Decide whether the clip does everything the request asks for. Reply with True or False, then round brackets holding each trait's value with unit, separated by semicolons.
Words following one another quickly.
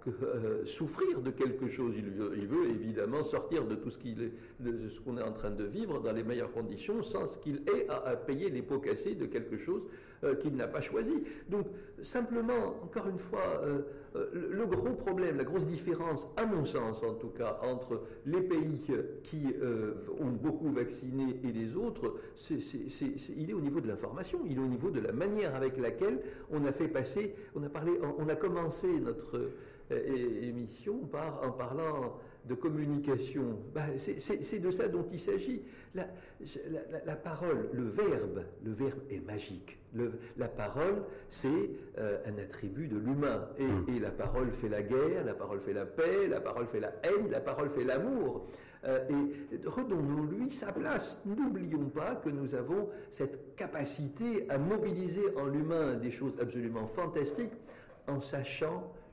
False (185 wpm)